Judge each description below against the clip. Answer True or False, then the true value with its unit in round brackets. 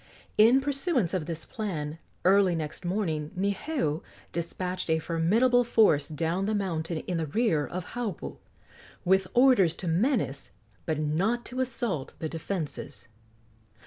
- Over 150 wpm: False (135 wpm)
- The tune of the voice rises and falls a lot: True (5.7 semitones)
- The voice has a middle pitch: True (180 Hz)